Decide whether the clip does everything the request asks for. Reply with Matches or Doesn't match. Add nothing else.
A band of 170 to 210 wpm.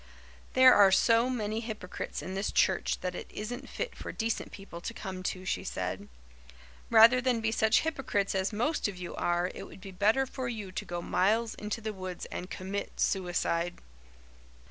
Matches